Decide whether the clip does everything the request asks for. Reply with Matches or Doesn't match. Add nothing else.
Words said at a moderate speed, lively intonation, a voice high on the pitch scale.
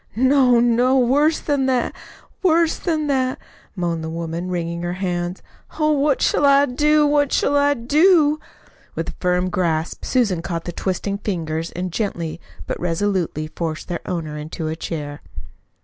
Matches